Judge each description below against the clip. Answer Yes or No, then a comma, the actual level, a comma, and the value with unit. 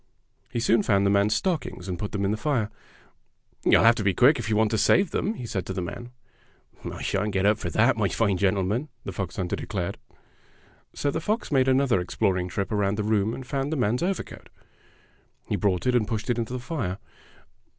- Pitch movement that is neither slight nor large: Yes, average, 4.3 semitones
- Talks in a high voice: No, low, 110 Hz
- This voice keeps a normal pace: No, fast, 225 wpm